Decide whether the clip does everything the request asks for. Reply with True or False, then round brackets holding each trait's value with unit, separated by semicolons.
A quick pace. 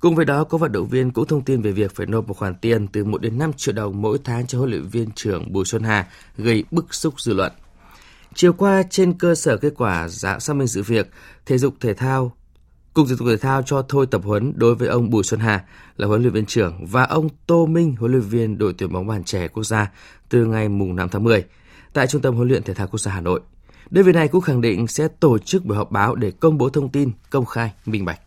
True (265 wpm)